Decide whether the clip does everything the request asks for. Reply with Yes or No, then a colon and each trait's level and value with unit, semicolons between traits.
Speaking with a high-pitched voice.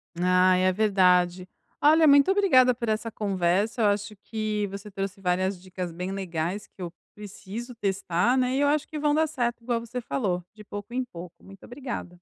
Yes: high, 205 Hz